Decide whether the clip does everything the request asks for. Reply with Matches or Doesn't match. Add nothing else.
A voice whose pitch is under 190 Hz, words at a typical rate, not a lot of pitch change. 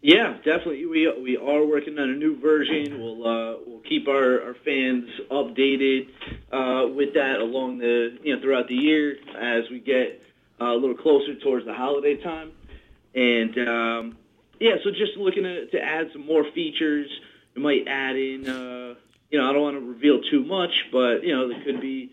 Doesn't match